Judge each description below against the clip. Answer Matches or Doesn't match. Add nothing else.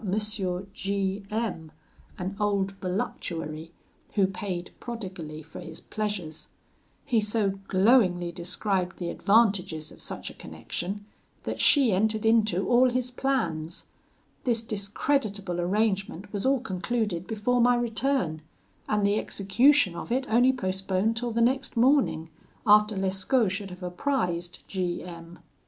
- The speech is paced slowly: Matches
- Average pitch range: Matches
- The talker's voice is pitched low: Doesn't match